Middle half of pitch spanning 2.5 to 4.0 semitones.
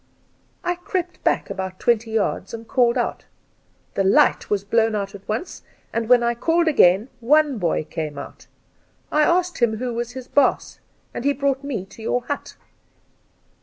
No: wide, 5.4 semitones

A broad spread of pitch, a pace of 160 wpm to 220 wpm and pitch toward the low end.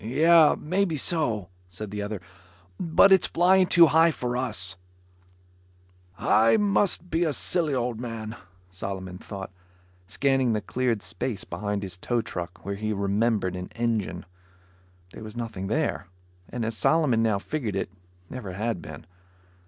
No: wide, 7.1 semitones; average, 145 wpm; low, 115 Hz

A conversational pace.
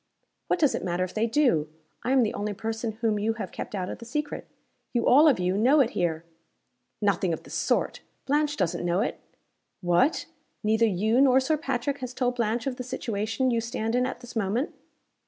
No: fast, 210 wpm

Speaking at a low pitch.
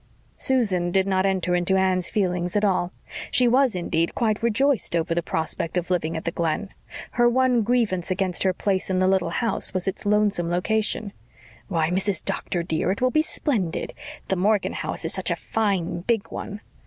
No: high, 190 Hz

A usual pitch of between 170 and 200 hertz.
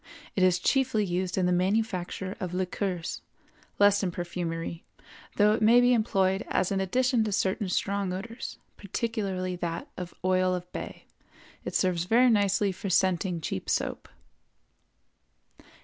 Yes: high, 190 Hz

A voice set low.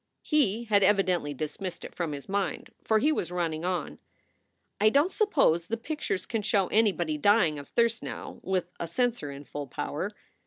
No: high, 190 Hz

